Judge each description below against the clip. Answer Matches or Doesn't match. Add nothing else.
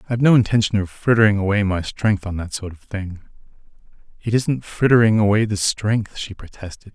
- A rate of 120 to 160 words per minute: Doesn't match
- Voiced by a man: Matches